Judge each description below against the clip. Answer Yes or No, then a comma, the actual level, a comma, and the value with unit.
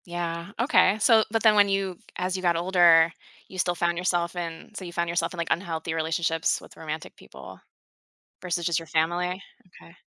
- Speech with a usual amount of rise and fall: No, narrow, 1.9 semitones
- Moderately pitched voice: Yes, medium, 175 Hz